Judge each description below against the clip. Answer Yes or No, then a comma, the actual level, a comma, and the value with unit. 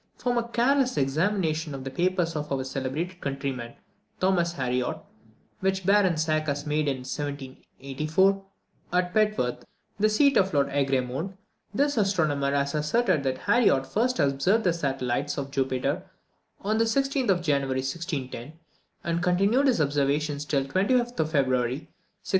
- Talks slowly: No, average, 145 wpm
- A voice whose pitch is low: No, medium, 155 Hz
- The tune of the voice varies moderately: No, wide, 6.1 semitones